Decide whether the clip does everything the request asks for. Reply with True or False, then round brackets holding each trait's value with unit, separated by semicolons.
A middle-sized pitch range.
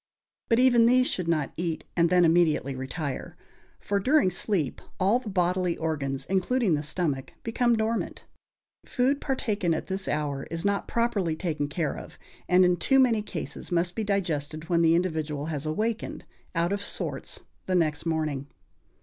True (5.0 semitones)